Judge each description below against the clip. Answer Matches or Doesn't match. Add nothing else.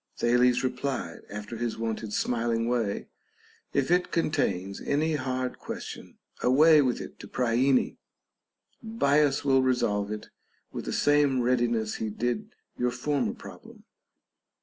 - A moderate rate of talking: Doesn't match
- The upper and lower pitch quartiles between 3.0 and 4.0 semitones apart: Matches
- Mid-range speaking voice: Doesn't match